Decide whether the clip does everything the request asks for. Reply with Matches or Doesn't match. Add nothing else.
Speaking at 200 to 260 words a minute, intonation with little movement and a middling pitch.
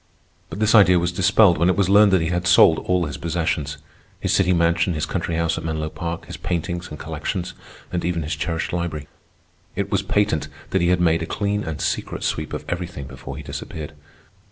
Doesn't match